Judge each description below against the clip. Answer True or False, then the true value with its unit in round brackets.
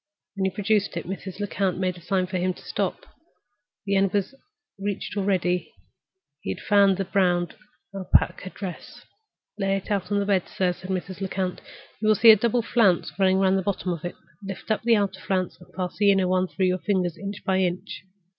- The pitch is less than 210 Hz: True (190 Hz)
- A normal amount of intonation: False (1.6 semitones)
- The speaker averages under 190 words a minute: False (205 wpm)